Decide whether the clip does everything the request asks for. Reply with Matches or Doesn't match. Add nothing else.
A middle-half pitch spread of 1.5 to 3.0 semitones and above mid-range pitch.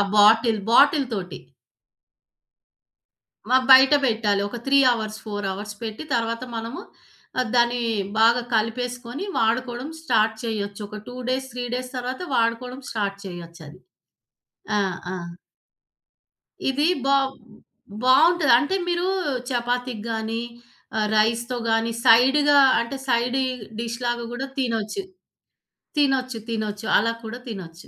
Matches